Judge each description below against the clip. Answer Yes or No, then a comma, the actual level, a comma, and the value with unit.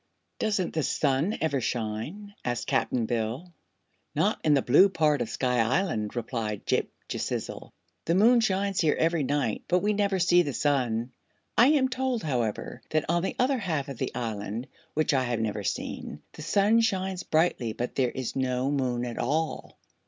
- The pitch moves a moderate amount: No, wide, 7.6 semitones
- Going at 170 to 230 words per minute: Yes, average, 175 wpm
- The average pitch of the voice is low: No, medium, 145 Hz